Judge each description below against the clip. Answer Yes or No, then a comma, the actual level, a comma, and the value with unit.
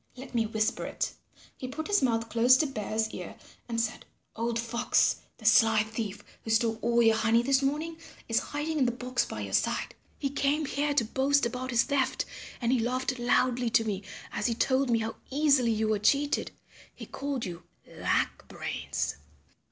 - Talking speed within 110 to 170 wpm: No, average, 190 wpm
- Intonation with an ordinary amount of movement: Yes, average, 3.3 semitones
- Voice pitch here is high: Yes, high, 240 Hz